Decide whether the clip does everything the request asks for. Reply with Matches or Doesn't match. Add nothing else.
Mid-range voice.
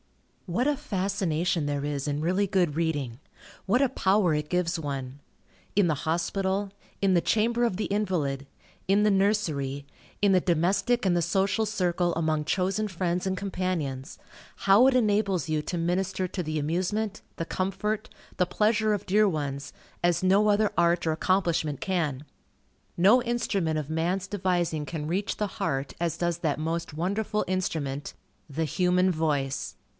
Matches